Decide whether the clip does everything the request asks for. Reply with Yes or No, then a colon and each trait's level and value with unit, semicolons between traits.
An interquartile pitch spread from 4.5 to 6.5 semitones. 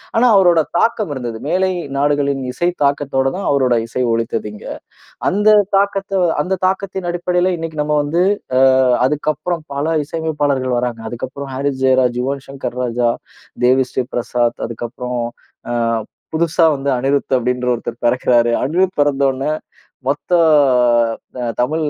Yes: average, 4.8 semitones